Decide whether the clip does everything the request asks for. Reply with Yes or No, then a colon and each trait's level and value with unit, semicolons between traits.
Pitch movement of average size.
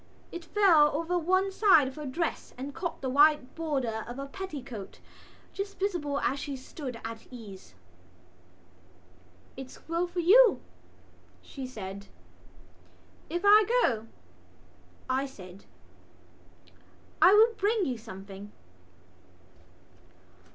No: wide, 6.6 semitones